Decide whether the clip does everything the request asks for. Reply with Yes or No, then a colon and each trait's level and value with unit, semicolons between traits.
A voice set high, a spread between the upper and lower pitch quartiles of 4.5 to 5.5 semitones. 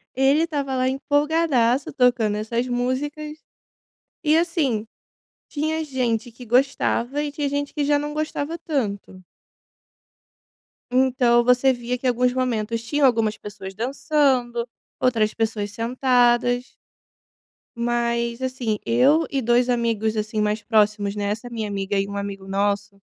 No: high, 245 Hz; average, 3.8 semitones